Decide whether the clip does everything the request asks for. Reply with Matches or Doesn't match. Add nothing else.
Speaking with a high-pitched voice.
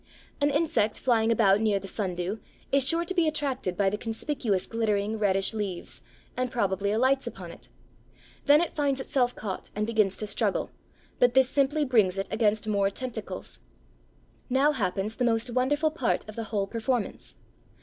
Matches